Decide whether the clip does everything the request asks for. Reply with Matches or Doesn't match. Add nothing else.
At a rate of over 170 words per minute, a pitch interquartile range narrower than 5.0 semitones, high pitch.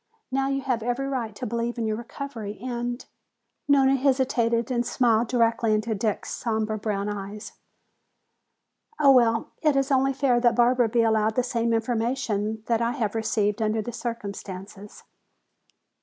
Doesn't match